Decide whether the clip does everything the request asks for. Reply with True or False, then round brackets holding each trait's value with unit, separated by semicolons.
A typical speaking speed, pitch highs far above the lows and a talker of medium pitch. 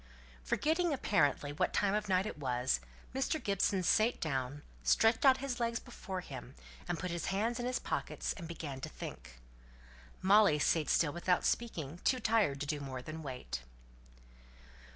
True (160 wpm; 7.7 semitones; 175 Hz)